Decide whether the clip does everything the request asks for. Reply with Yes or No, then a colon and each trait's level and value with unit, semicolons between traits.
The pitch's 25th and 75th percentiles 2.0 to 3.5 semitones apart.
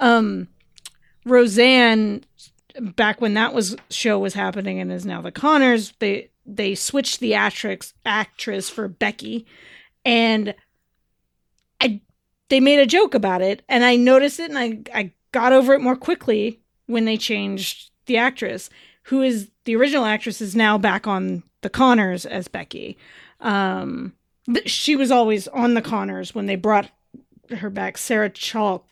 Yes: average, 3.2 semitones